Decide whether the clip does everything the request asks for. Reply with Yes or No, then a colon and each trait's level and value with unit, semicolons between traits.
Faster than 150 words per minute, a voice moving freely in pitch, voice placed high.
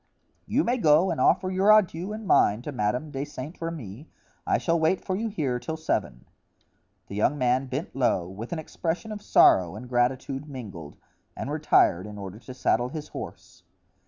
No: average, 185 wpm; wide, 5.8 semitones; low, 135 Hz